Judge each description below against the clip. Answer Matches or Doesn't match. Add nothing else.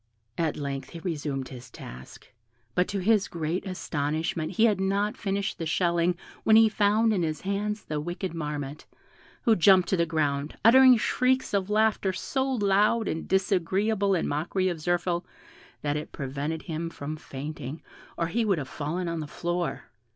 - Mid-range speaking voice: Matches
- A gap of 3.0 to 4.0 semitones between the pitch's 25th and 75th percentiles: Doesn't match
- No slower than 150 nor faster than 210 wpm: Matches